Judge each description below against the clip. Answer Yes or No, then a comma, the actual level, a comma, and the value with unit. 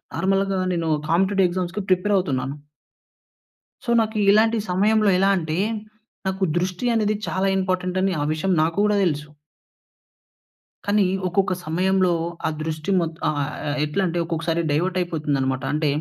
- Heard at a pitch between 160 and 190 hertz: Yes, medium, 185 Hz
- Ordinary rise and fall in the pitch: Yes, average, 3.3 semitones